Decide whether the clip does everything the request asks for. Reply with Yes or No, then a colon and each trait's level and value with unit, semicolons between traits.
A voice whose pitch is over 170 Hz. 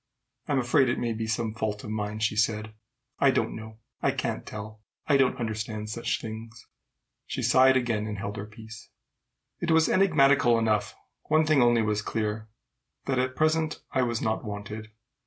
No: low, 110 Hz